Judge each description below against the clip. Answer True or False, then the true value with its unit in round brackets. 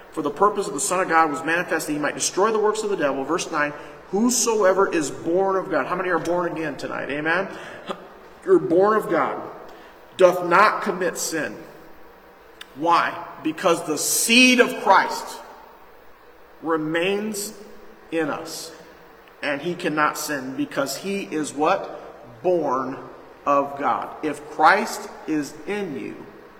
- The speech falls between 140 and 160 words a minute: True (150 wpm)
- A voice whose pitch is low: False (180 Hz)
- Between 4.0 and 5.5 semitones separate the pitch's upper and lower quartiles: True (4.9 semitones)